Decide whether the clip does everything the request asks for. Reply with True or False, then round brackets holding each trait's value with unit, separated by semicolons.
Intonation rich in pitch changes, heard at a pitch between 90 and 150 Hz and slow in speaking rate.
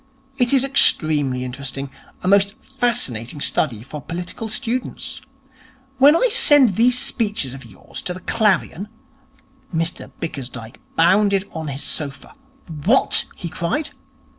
False (9.0 semitones; 180 Hz; 130 wpm)